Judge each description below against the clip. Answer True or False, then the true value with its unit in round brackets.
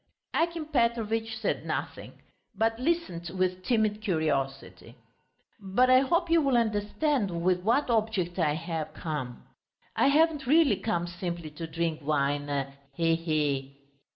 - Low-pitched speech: False (190 Hz)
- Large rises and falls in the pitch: True (7.2 semitones)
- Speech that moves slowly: True (130 wpm)